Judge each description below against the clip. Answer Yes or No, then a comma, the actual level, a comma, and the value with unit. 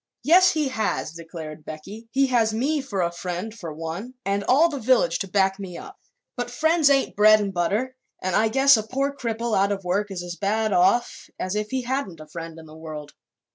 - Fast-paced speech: Yes, fast, 215 wpm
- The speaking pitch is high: Yes, high, 210 Hz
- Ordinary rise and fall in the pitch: No, wide, 6.5 semitones